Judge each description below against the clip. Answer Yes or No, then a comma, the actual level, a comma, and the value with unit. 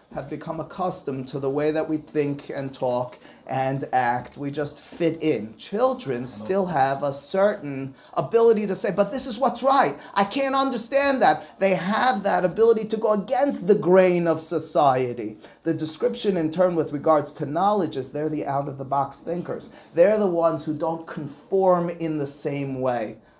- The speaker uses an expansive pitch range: Yes, wide, 6.0 semitones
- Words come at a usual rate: Yes, average, 180 wpm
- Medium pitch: Yes, medium, 160 Hz